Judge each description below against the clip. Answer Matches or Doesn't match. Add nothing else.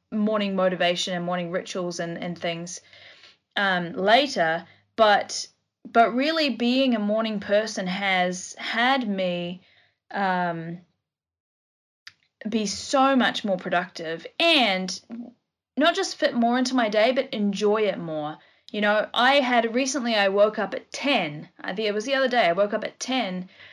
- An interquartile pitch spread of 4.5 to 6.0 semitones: Matches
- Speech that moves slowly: Doesn't match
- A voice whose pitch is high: Matches